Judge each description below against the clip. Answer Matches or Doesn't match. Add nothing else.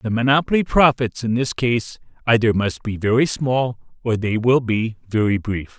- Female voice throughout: Doesn't match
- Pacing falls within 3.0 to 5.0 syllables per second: Matches